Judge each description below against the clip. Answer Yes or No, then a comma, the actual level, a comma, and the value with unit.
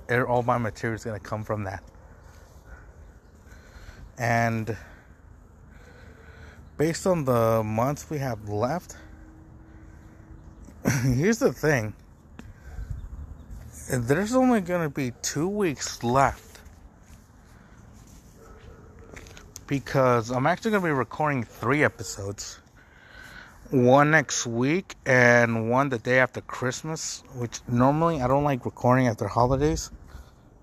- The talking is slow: Yes, slow, 105 wpm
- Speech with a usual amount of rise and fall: No, wide, 7.3 semitones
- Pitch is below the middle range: Yes, low, 115 Hz